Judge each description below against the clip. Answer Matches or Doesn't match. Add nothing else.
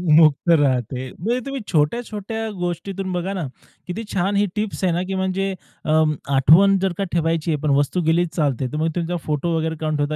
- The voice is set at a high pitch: Doesn't match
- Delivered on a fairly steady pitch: Doesn't match